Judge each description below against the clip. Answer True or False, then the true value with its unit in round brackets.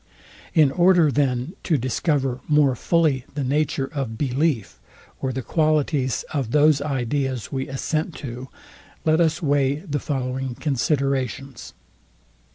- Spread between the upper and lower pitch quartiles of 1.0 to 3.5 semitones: True (2.7 semitones)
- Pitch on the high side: False (140 Hz)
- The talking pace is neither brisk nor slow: False (125 wpm)